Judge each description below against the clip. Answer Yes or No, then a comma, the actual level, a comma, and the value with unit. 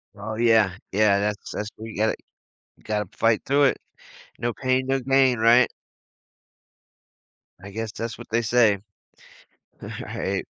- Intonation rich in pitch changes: No, narrow, 2.6 semitones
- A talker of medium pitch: No, low, 115 Hz